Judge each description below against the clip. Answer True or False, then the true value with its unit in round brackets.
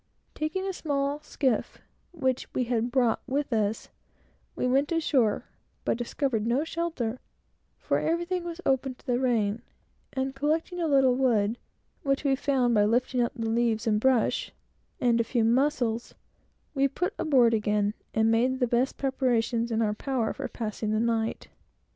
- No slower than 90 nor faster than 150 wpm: False (160 wpm)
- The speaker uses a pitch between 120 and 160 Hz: False (250 Hz)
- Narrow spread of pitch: False (3.5 semitones)